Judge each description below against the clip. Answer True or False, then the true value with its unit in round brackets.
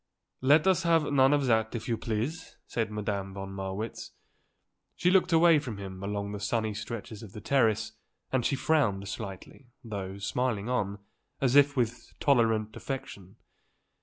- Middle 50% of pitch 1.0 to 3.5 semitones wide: False (4.9 semitones)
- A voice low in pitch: True (110 Hz)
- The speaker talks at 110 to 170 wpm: True (160 wpm)